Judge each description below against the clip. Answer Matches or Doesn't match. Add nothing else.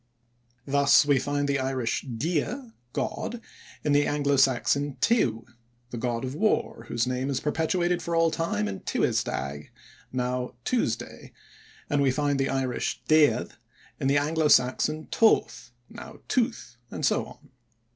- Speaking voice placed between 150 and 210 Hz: Doesn't match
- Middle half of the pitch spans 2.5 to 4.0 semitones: Matches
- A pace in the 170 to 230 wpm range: Doesn't match